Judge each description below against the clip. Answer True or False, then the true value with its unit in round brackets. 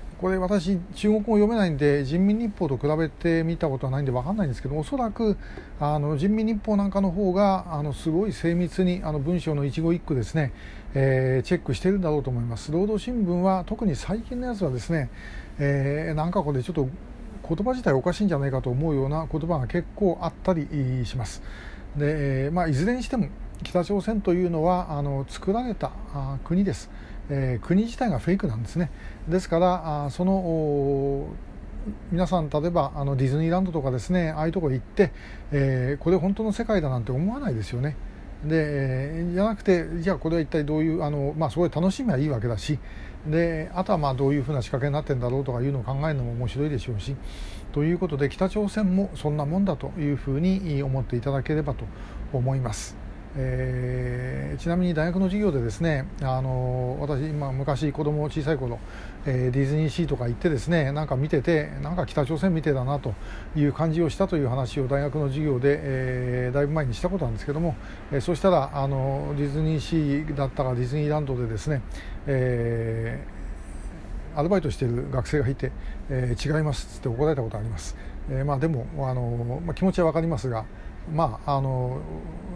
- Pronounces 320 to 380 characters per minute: False (395 characters per minute)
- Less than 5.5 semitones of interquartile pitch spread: True (5.1 semitones)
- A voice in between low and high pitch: True (150 Hz)